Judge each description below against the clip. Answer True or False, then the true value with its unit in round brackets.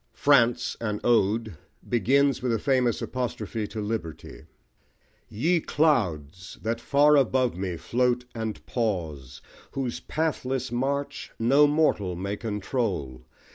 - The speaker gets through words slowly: True (115 wpm)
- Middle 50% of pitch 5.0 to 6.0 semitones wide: False (4.6 semitones)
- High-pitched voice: False (115 Hz)